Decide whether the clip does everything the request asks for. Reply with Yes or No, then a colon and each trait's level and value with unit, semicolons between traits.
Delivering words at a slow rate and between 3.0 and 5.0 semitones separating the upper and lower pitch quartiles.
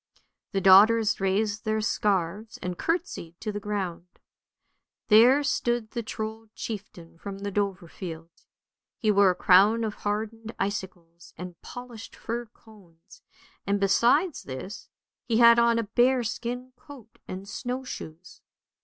Yes: slow, 130 wpm; average, 3.6 semitones